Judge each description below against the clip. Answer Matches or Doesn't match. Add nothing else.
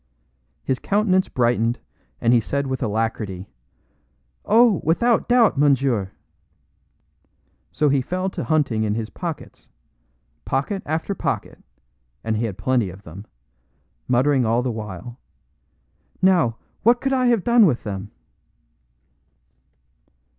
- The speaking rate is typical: Doesn't match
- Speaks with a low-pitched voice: Matches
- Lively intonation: Matches